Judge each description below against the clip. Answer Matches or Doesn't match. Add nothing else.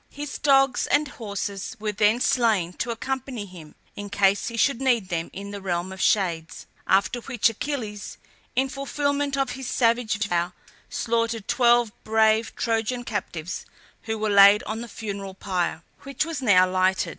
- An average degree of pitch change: Matches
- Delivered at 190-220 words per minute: Doesn't match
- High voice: Matches